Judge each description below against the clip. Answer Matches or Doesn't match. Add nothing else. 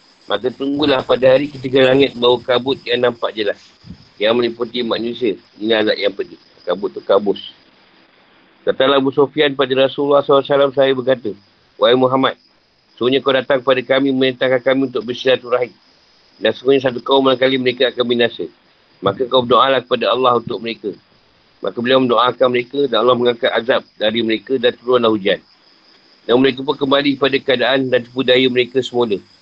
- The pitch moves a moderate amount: Doesn't match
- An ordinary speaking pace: Doesn't match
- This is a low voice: Matches